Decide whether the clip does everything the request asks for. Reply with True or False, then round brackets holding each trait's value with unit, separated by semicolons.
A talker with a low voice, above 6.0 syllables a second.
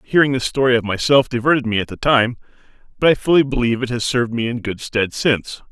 True (125 Hz; 6.5 syllables/s)